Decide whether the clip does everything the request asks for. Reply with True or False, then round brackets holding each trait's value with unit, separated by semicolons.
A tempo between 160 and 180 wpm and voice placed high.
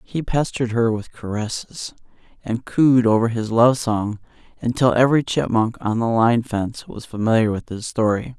False (165 wpm; 115 Hz)